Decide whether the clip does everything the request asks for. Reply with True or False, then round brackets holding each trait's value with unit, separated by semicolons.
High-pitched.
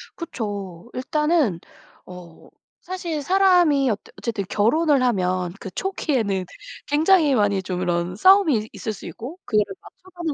True (245 Hz)